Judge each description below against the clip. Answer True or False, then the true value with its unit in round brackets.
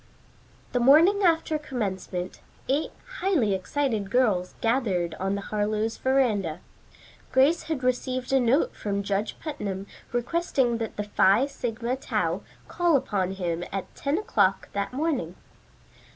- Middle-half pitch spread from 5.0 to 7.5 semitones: True (5.6 semitones)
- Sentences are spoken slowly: True (130 wpm)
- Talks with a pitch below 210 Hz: False (235 Hz)